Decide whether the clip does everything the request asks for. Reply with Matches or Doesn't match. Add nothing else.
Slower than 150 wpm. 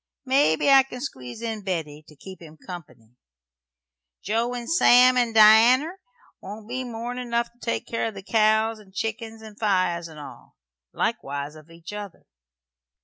Doesn't match